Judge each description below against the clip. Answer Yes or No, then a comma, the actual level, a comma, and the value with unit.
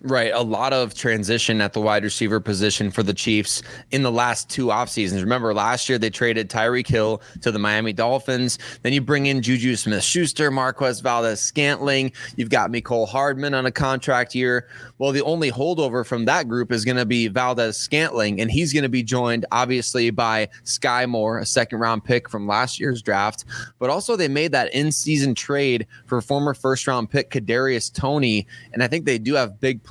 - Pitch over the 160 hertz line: No, low, 125 Hz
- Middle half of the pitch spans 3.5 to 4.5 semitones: No, average, 3.0 semitones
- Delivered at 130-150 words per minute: No, average, 190 wpm